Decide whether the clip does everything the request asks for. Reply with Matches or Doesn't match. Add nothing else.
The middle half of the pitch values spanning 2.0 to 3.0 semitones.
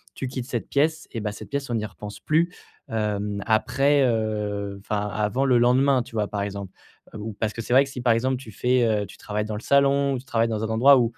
Doesn't match